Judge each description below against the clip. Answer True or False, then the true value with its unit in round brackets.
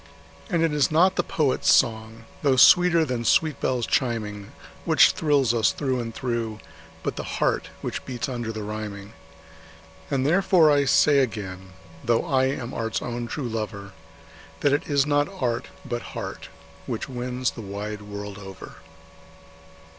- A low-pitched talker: True (120 Hz)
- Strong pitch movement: False (4.4 semitones)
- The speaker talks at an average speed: True (155 wpm)